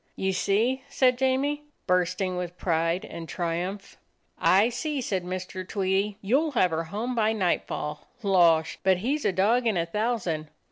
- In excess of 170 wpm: No, average, 160 wpm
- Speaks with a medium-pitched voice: No, high, 195 Hz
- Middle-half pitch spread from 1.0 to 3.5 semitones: No, average, 5.0 semitones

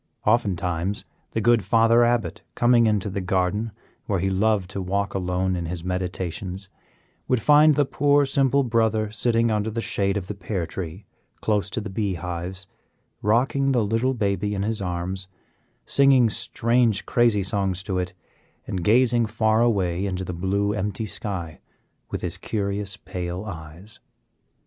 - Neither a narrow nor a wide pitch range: Yes, average, 3.6 semitones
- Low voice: Yes, low, 100 Hz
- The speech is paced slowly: No, average, 155 wpm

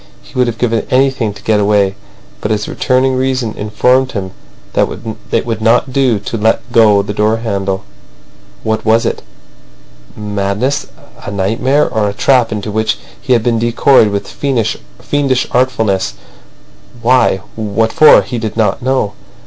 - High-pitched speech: No, low, 110 Hz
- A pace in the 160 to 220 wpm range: No, average, 150 wpm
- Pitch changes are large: No, average, 3.6 semitones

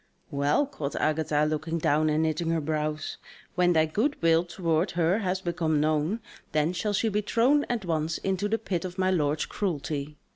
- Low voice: No, medium, 165 Hz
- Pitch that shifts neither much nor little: Yes, average, 3.6 semitones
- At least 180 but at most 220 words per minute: Yes, average, 185 wpm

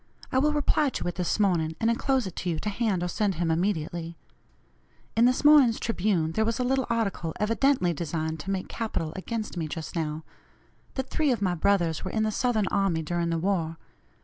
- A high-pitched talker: Yes, high, 195 Hz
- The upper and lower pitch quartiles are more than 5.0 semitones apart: Yes, wide, 5.6 semitones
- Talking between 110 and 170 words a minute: No, fast, 205 wpm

